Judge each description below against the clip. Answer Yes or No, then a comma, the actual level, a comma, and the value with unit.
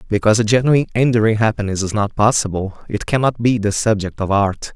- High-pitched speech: No, low, 110 Hz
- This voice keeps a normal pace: Yes, average, 190 wpm